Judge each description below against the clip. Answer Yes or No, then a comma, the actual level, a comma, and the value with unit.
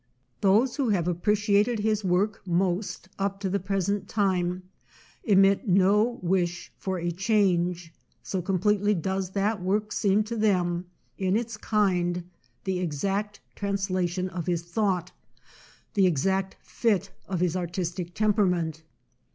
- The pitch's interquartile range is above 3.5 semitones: No, narrow, 2.6 semitones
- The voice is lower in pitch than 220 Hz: Yes, high, 190 Hz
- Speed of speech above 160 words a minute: No, slow, 135 wpm